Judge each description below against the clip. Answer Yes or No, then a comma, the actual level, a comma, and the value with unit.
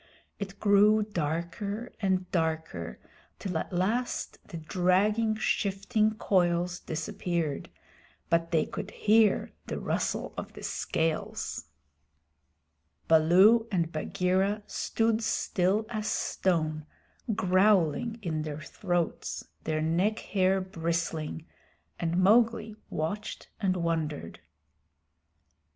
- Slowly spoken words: Yes, slow, 100 wpm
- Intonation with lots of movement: No, average, 4.3 semitones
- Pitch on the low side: No, medium, 185 Hz